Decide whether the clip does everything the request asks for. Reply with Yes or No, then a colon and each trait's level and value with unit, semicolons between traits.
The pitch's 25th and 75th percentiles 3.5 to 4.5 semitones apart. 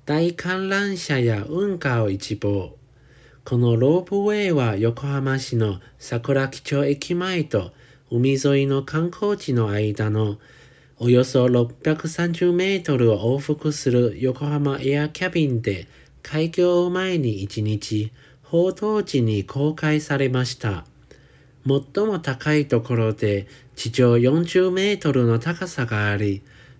No: wide, 5.6 semitones